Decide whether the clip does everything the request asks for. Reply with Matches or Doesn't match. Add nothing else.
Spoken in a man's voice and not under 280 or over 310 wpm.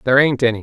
Matches